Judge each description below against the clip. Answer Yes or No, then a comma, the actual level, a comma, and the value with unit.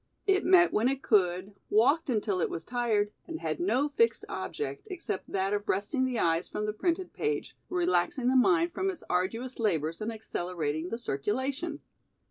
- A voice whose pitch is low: No, high, 240 Hz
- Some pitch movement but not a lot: No, wide, 9.0 semitones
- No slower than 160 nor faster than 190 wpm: Yes, average, 175 wpm